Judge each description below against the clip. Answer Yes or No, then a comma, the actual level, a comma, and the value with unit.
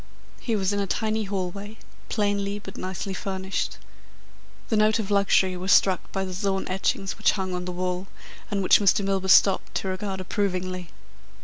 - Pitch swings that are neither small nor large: No, narrow, 1.5 semitones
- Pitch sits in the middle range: No, high, 195 Hz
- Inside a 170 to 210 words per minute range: Yes, average, 175 wpm